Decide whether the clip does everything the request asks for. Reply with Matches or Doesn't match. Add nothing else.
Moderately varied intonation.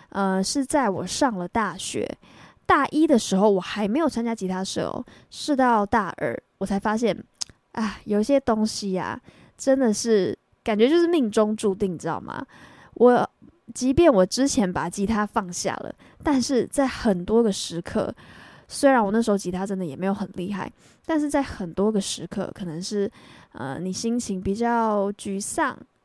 Matches